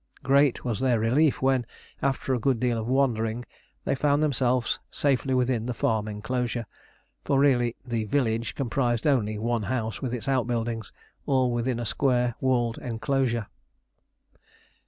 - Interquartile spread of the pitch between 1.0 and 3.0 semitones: Yes, narrow, 2.4 semitones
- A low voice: Yes, low, 125 Hz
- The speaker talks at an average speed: Yes, average, 145 wpm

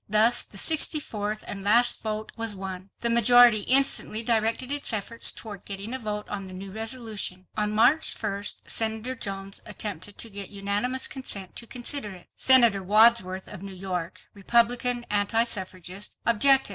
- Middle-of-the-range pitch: No, high, 215 Hz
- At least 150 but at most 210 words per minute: Yes, average, 160 wpm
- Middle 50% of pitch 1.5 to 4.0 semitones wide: Yes, average, 3.1 semitones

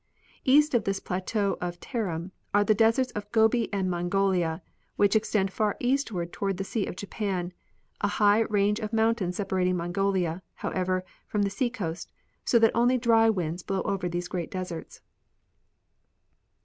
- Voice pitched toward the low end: No, high, 200 Hz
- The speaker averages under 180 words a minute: Yes, average, 160 wpm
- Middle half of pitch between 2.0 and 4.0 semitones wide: Yes, average, 3.5 semitones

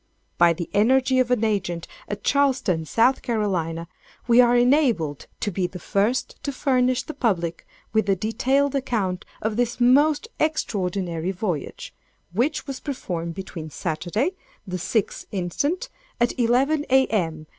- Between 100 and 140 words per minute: Yes, slow, 135 wpm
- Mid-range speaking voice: No, high, 220 Hz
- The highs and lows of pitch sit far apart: Yes, wide, 6.4 semitones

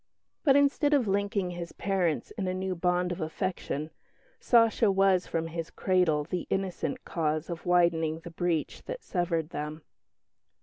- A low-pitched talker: No, medium, 180 Hz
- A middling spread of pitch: Yes, average, 3.0 semitones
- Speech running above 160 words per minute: No, average, 150 wpm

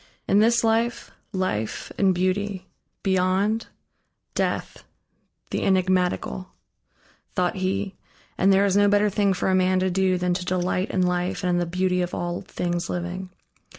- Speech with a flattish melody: Yes, narrow, 1.6 semitones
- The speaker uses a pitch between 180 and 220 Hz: Yes, medium, 185 Hz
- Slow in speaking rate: No, average, 155 wpm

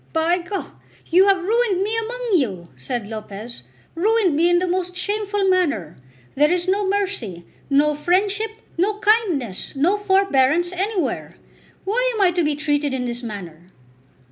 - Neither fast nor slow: Yes, average, 155 wpm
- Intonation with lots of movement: Yes, wide, 6.8 semitones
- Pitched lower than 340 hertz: No, very high, 355 Hz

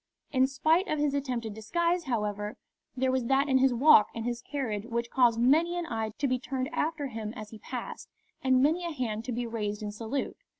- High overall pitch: Yes, very high, 255 Hz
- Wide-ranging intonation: No, average, 4.0 semitones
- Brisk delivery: Yes, fast, 215 wpm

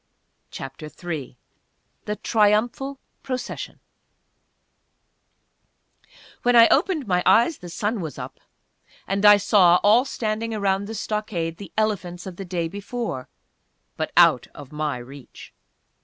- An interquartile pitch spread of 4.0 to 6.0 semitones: Yes, average, 4.7 semitones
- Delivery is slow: Yes, slow, 125 wpm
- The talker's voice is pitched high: Yes, high, 200 Hz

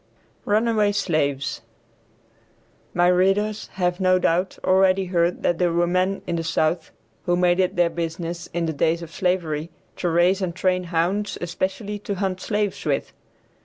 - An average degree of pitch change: No, narrow, 2.1 semitones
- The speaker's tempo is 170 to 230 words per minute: No, average, 160 wpm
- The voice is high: No, medium, 180 Hz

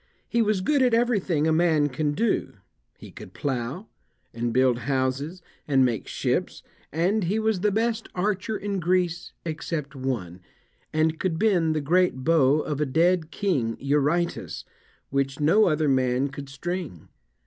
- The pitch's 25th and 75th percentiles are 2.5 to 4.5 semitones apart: No, average, 5.3 semitones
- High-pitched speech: No, medium, 160 Hz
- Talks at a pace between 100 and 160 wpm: Yes, average, 155 wpm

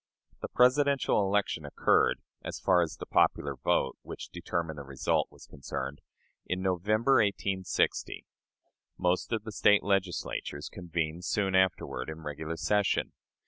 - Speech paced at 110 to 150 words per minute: Yes, slow, 135 wpm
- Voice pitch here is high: No, very low, 90 Hz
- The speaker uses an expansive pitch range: No, average, 4.6 semitones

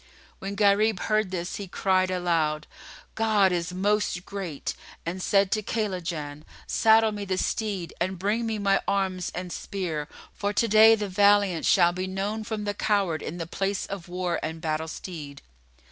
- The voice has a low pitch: No, high, 190 Hz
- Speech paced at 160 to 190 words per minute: Yes, average, 170 wpm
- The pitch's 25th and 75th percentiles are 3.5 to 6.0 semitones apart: No, average, 2.8 semitones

